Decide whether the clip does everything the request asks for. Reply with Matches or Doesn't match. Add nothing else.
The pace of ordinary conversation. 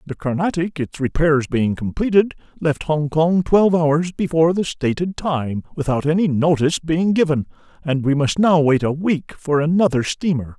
Matches